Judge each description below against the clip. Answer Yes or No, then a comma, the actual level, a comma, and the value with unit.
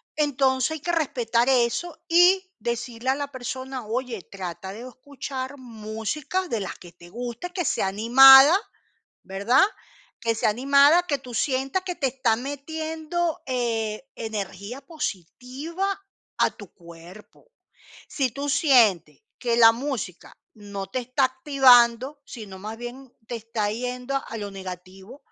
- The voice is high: Yes, very high, 250 Hz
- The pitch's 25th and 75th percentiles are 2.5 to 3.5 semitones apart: No, average, 4.3 semitones